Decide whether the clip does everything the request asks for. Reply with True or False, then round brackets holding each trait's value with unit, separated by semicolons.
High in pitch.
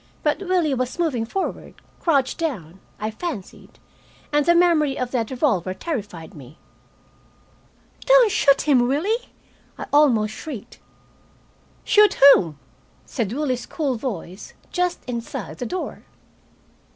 True (270 Hz)